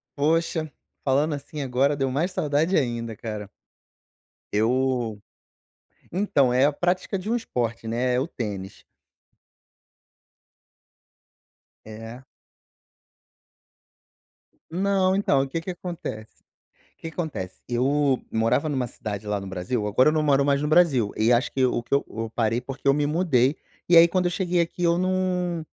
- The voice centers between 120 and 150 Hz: Yes, medium, 140 Hz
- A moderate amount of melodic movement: No, wide, 6.1 semitones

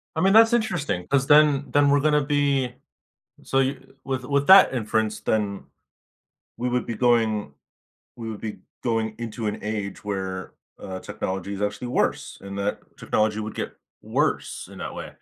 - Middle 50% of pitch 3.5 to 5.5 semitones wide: Yes, average, 5.2 semitones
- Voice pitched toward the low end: Yes, low, 115 Hz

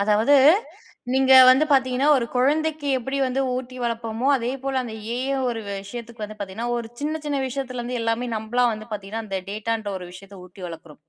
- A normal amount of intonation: Yes, average, 3.5 semitones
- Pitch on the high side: Yes, high, 240 Hz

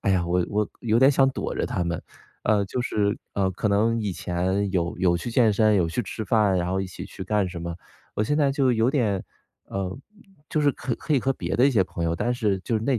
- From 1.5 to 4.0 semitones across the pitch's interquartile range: No, average, 4.4 semitones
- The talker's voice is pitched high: No, low, 105 Hz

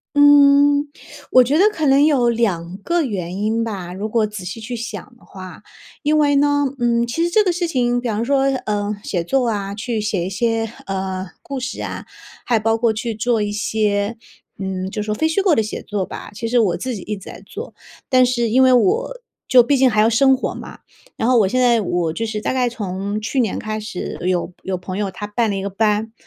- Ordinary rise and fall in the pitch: Yes, average, 4.1 semitones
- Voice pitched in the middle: No, high, 225 Hz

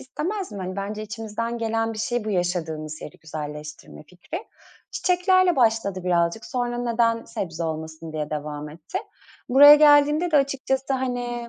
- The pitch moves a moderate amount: No, wide, 7.9 semitones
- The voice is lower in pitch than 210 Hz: No, high, 225 Hz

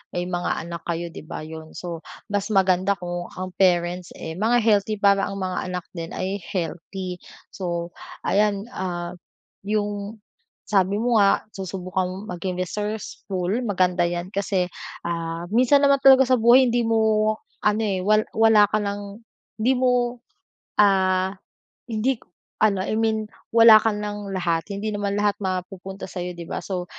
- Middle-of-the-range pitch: No, high, 195 Hz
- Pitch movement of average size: Yes, average, 3.0 semitones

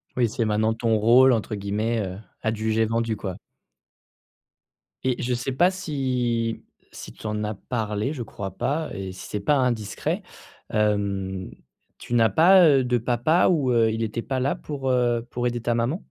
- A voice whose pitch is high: No, low, 115 Hz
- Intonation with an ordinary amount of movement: Yes, average, 3.2 semitones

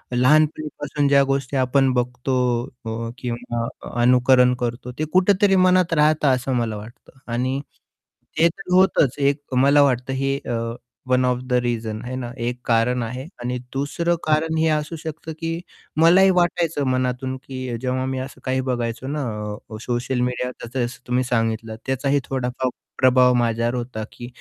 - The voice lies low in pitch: Yes, low, 130 Hz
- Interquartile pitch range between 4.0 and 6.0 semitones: No, average, 2.9 semitones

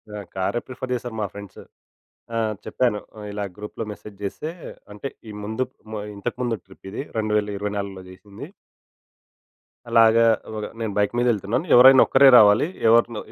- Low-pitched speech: Yes, low, 105 Hz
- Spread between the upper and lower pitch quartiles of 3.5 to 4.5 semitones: No, average, 2.8 semitones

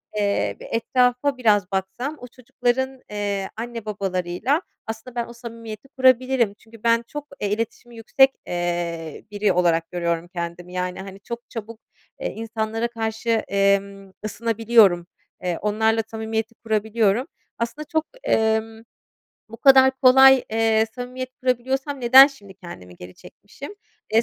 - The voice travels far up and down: No, average, 3.8 semitones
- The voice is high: Yes, high, 225 Hz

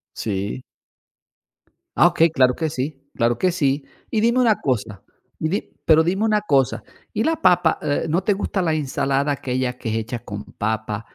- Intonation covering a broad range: Yes, wide, 6.6 semitones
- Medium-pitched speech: Yes, medium, 145 Hz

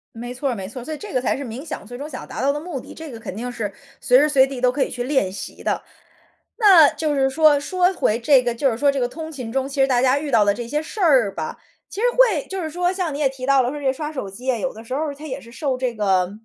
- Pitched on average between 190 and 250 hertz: No, very high, 270 Hz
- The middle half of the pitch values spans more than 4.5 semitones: No, average, 3.8 semitones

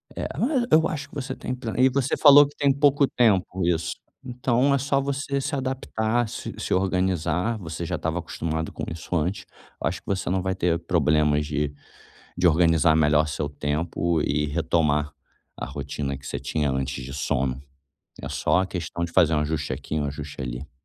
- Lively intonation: Yes, wide, 8.5 semitones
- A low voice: Yes, very low, 85 Hz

